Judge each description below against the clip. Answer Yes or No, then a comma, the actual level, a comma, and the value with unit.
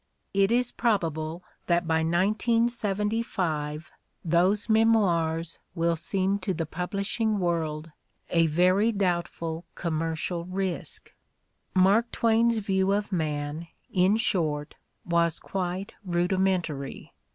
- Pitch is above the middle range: No, medium, 180 Hz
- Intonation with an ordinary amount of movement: Yes, average, 3.5 semitones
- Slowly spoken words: Yes, slow, 105 wpm